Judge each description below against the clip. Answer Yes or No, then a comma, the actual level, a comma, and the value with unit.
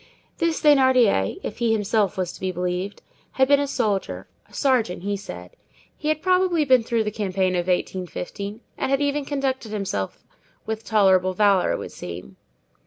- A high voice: Yes, high, 210 Hz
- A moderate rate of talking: Yes, average, 170 wpm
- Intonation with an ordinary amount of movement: No, wide, 6.1 semitones